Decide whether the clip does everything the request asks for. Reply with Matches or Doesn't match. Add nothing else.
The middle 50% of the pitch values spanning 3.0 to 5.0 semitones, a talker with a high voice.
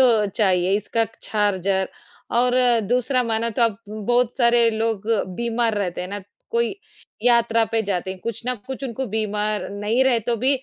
Doesn't match